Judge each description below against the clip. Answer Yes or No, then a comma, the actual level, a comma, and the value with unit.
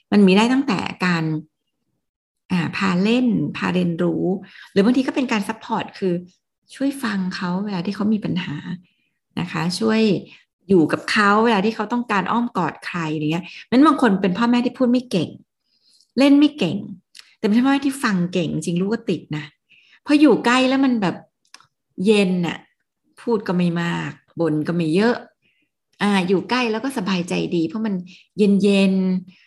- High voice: Yes, high, 200 Hz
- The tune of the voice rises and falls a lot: No, average, 4.7 semitones